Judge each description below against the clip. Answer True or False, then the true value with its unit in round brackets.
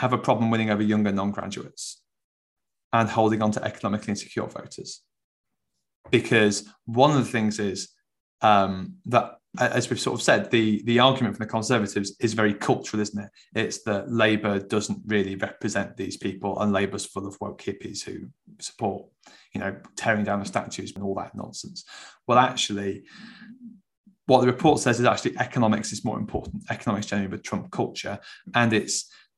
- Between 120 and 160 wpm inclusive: False (170 wpm)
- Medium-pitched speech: False (105 Hz)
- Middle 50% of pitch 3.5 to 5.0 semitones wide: False (2.9 semitones)